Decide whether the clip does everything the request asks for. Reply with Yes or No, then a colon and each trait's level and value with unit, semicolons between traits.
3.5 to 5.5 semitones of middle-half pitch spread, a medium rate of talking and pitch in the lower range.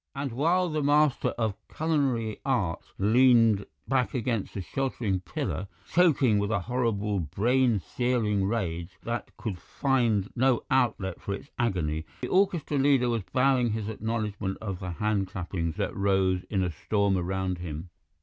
Yes: average, 5.1 semitones; average, 150 wpm; low, 110 Hz